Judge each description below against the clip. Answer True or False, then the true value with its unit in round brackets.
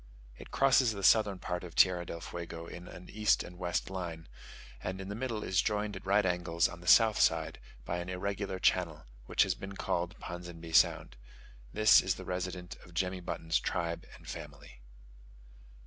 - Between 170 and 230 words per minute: True (180 wpm)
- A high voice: False (90 Hz)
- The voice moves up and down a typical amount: False (2.2 semitones)